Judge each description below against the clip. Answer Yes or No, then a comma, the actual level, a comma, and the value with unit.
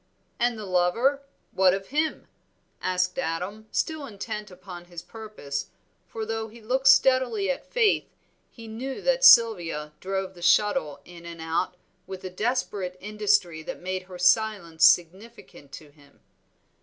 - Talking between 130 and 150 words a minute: Yes, average, 145 wpm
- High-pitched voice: Yes, high, 195 Hz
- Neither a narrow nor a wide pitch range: Yes, average, 4.6 semitones